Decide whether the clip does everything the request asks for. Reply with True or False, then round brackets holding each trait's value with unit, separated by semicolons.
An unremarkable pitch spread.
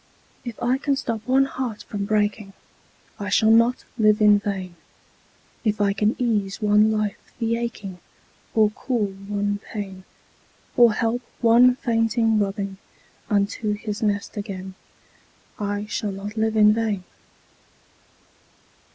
False (2.0 semitones)